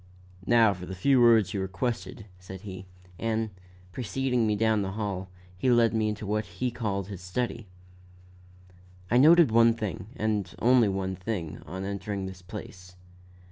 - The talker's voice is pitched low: Yes, low, 105 Hz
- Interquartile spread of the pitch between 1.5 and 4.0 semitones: Yes, average, 3.5 semitones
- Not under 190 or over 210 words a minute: No, average, 160 wpm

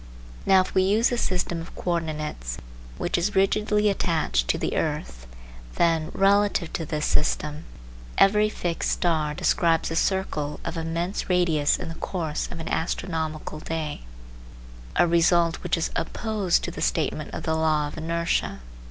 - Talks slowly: No, average, 160 wpm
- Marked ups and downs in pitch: No, average, 3.2 semitones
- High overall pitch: No, medium, 165 Hz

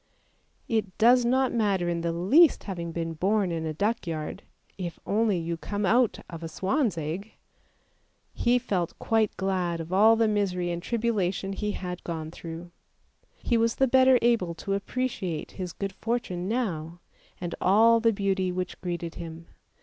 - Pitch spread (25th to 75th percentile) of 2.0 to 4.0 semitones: No, average, 4.8 semitones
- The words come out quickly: No, average, 165 wpm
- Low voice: No, high, 190 Hz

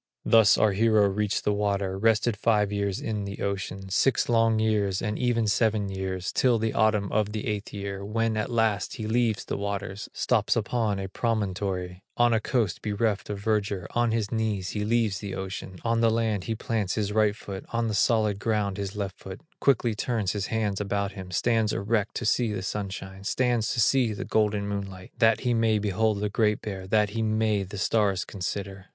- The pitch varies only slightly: Yes, narrow, 2.1 semitones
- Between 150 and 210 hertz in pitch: No, low, 105 Hz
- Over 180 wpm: Yes, average, 200 wpm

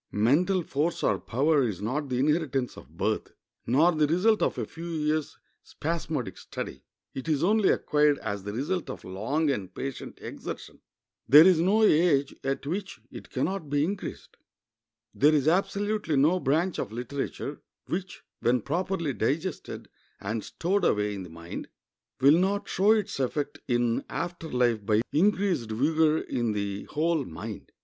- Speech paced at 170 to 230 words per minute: No, average, 160 wpm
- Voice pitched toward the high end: No, medium, 150 Hz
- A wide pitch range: Yes, wide, 6.0 semitones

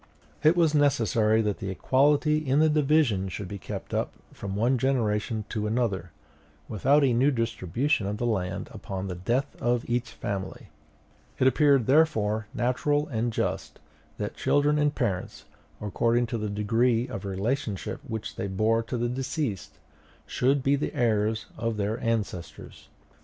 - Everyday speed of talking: Yes, average, 155 wpm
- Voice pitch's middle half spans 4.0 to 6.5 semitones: Yes, average, 4.6 semitones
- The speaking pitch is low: Yes, low, 115 Hz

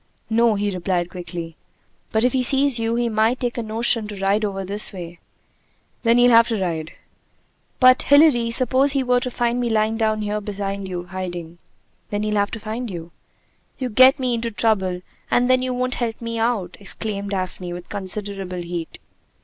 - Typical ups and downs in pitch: Yes, average, 4.1 semitones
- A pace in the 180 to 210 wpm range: Yes, average, 190 wpm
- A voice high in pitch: Yes, high, 215 Hz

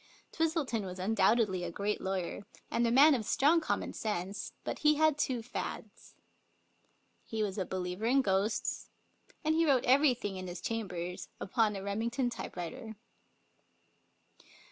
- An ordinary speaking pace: Yes, average, 145 wpm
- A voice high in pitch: Yes, high, 220 Hz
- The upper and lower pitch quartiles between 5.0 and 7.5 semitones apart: Yes, wide, 5.4 semitones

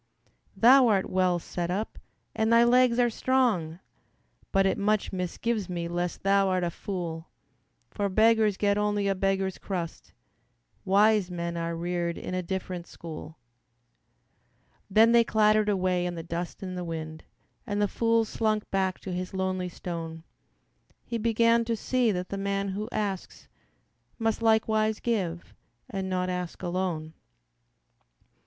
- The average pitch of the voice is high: Yes, high, 195 Hz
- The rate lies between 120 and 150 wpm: Yes, average, 145 wpm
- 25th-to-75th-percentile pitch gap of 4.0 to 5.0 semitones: No, average, 3.5 semitones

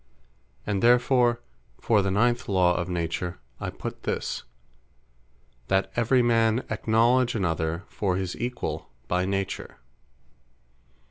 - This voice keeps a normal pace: No, slow, 115 wpm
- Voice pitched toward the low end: Yes, low, 100 Hz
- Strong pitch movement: No, average, 4.7 semitones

